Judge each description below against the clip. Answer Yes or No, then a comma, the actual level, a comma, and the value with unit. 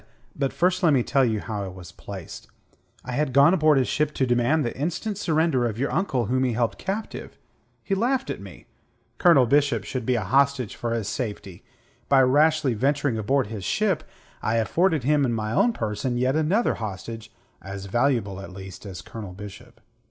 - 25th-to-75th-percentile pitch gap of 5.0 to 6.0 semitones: Yes, wide, 5.6 semitones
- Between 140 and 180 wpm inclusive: No, average, 190 wpm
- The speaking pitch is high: No, low, 125 Hz